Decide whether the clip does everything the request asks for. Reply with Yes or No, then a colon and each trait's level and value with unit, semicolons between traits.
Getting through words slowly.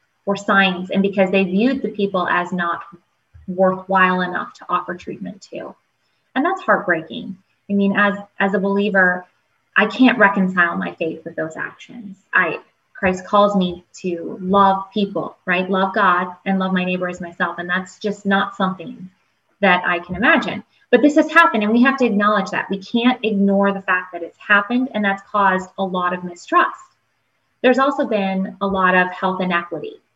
No: average, 180 wpm